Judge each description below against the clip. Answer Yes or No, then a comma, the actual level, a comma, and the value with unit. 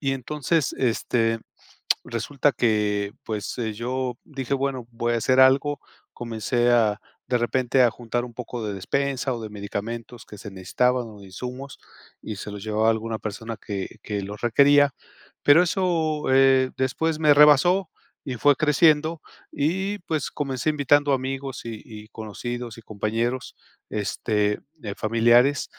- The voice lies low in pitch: Yes, low, 125 Hz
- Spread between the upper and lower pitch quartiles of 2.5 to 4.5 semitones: Yes, average, 4.0 semitones